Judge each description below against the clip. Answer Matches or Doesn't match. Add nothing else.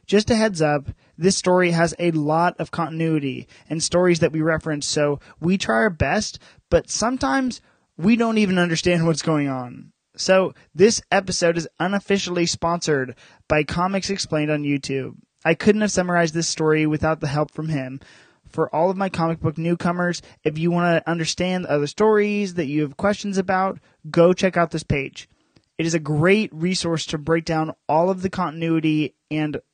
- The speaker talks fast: Doesn't match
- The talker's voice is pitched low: Doesn't match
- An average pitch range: Matches